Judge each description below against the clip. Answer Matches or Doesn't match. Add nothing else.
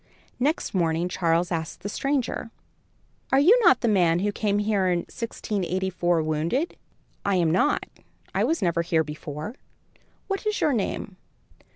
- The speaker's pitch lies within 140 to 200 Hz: Matches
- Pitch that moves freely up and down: Matches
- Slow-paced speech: Doesn't match